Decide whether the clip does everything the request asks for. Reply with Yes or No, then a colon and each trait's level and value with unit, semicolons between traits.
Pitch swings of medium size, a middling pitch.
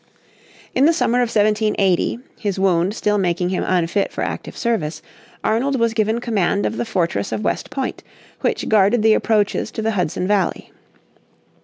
No: average, 3.3 semitones; high, 210 Hz